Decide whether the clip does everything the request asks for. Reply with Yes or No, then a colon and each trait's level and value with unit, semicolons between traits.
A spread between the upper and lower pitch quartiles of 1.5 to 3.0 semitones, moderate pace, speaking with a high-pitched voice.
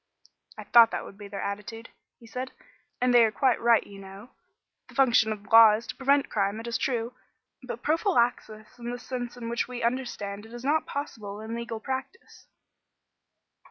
Yes: narrow, 2.6 semitones; average, 190 wpm; high, 235 Hz